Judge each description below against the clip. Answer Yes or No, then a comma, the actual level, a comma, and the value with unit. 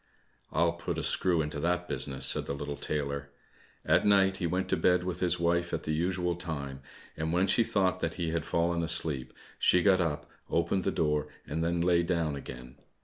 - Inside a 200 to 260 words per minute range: Yes, fast, 205 wpm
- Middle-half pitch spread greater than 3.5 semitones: No, average, 2.8 semitones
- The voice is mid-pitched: No, very low, 85 Hz